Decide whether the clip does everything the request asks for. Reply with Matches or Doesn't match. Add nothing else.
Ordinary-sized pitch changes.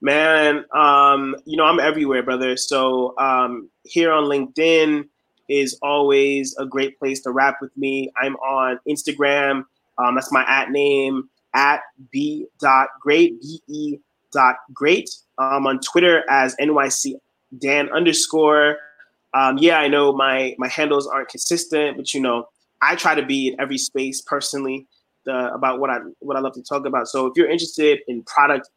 Doesn't match